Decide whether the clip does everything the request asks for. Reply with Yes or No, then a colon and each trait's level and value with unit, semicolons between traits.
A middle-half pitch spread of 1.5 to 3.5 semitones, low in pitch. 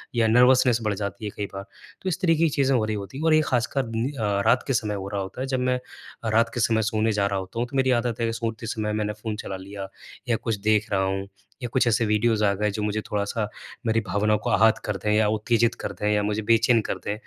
Yes: narrow, 2.5 semitones; low, 110 Hz